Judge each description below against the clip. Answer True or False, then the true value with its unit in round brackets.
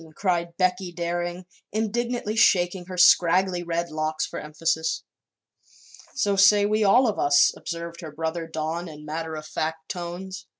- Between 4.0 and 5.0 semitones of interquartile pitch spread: False (2.9 semitones)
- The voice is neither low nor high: True (175 Hz)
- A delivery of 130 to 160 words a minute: True (145 wpm)